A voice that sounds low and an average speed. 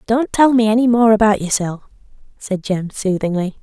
No: high, 210 Hz; average, 165 wpm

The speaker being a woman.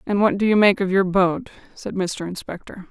Yes: female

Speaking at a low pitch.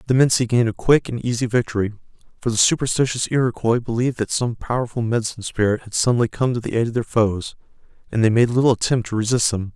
Yes: low, 115 Hz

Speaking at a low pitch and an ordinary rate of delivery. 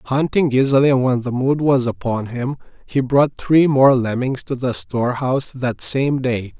Yes: low, 130 Hz; average, 180 wpm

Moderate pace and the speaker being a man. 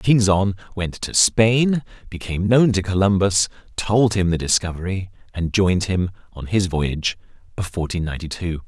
Yes: average, 150 wpm; male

